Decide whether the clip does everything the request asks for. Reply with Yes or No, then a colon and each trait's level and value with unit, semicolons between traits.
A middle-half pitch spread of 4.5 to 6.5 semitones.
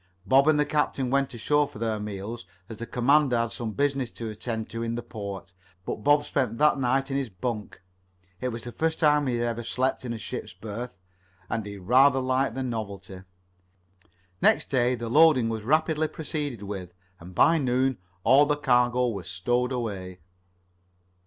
No: average, 3.9 semitones